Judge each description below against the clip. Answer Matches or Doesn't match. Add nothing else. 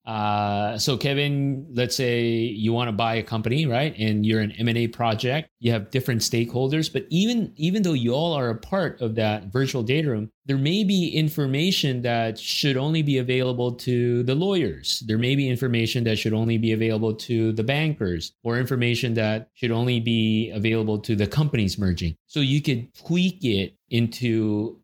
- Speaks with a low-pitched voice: Matches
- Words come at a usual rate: Matches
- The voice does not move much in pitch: Doesn't match